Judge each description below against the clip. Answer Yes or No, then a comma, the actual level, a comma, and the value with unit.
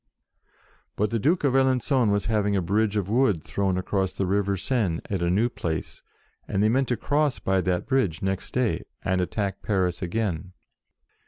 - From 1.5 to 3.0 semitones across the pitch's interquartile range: No, average, 4.2 semitones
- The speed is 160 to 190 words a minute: Yes, average, 180 wpm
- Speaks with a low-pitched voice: Yes, low, 100 Hz